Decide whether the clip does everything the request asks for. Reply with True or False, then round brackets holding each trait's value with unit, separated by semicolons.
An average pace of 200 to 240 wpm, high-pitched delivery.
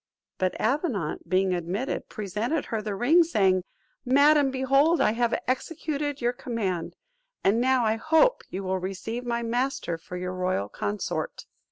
False (150 wpm; 230 Hz)